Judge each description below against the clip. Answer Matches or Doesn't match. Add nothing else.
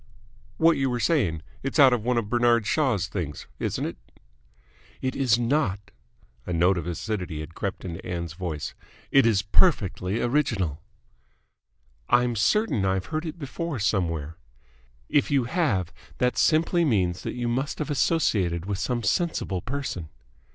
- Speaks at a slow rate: Doesn't match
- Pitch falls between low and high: Doesn't match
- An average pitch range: Doesn't match